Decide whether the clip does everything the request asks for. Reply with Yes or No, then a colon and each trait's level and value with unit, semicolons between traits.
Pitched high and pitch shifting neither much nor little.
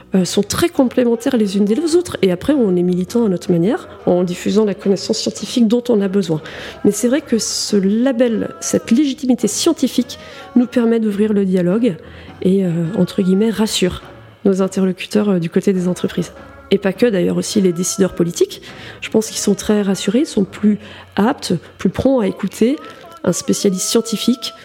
Yes: high, 210 Hz; average, 4.0 semitones